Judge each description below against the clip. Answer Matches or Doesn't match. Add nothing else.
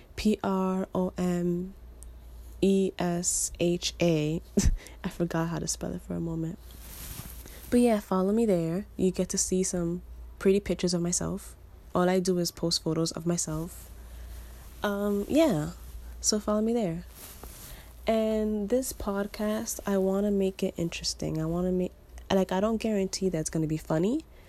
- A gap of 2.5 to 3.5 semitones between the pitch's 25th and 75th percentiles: Matches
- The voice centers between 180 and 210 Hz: Matches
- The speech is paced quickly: Doesn't match